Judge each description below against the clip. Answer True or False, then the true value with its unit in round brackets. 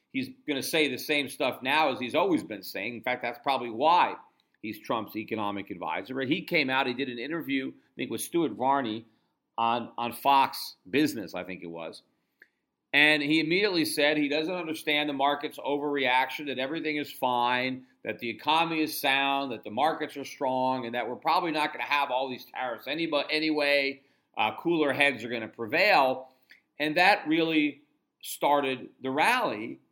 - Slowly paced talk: False (185 wpm)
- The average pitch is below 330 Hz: True (140 Hz)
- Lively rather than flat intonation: False (3.7 semitones)